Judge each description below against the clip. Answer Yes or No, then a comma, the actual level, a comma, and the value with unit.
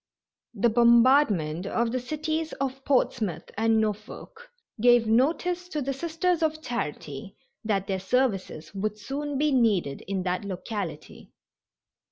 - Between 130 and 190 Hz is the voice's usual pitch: No, high, 235 Hz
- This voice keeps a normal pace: No, slow, 130 wpm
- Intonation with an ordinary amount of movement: No, wide, 6.4 semitones